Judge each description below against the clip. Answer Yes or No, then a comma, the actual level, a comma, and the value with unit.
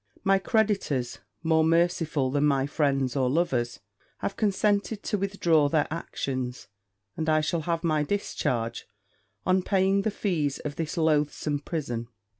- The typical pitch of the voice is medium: Yes, medium, 155 Hz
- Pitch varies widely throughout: No, average, 4.8 semitones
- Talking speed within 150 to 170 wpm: No, average, 140 wpm